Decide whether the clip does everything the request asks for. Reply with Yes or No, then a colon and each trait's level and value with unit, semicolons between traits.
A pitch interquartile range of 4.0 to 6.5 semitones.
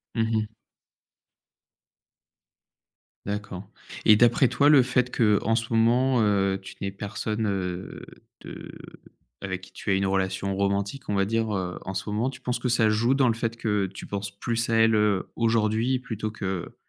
No: average, 2.9 semitones